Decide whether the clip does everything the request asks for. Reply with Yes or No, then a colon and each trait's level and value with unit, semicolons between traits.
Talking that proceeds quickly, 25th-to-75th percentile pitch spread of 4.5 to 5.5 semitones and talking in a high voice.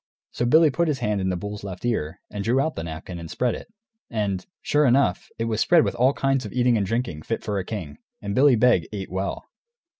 No: fast, 240 wpm; average, 5.0 semitones; low, 110 Hz